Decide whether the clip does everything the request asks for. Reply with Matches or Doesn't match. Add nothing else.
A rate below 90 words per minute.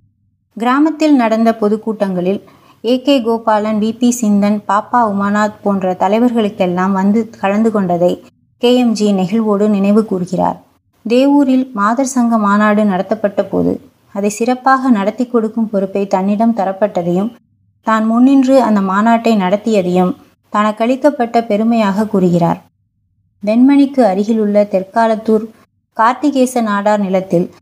Doesn't match